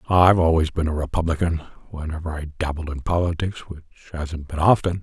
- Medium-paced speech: Yes, average, 165 wpm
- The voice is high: No, very low, 80 Hz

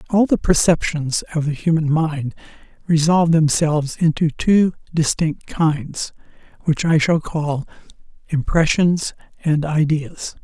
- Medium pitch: Yes, medium, 160 Hz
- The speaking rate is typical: No, slow, 115 wpm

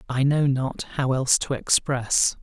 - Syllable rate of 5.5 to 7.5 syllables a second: No, 4.0 syllables/s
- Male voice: Yes, male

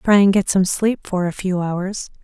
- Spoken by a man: No, female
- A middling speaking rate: No, fast, 240 wpm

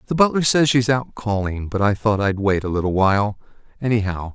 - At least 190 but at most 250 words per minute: Yes, fast, 205 wpm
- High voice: No, low, 110 Hz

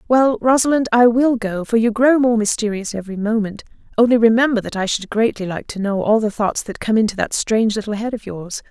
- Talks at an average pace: No, fast, 225 wpm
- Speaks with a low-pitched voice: No, high, 225 Hz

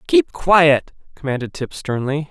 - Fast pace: No, slow, 130 wpm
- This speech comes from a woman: No, male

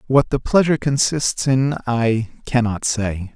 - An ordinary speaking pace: Yes, average, 145 wpm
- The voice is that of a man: Yes, male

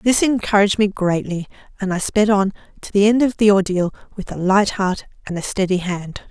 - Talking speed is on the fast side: Yes, fast, 210 wpm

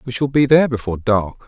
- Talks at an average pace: No, fast, 245 wpm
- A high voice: No, low, 125 Hz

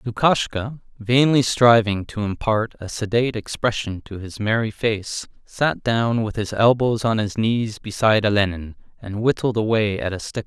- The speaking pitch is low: Yes, low, 110 Hz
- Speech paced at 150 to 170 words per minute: Yes, average, 160 wpm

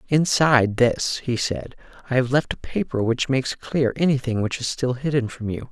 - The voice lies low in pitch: Yes, low, 125 Hz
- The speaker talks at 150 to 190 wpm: No, average, 200 wpm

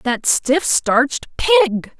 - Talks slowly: Yes, slow, 120 wpm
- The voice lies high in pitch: Yes, very high, 285 Hz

